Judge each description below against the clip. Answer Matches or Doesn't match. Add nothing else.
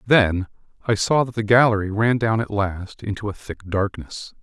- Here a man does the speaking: Matches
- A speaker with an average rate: Matches